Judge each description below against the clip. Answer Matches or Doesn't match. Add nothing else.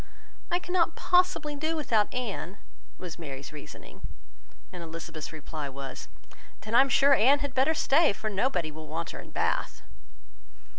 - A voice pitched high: Matches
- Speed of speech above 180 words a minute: Doesn't match